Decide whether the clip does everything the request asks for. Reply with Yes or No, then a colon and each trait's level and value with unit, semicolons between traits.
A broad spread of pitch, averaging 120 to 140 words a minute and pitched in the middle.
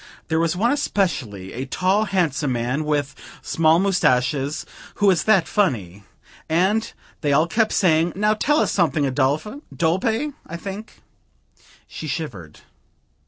Yes: wide, 6.2 semitones; slow, 135 wpm; medium, 165 Hz